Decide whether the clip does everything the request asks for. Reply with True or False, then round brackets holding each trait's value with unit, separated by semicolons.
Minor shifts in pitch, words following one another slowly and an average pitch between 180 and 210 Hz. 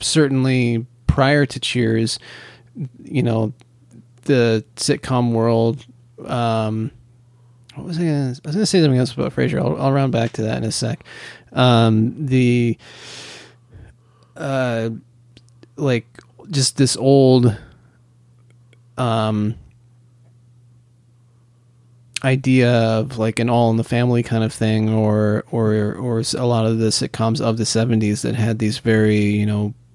False (1.9 semitones; 130 wpm; 120 Hz)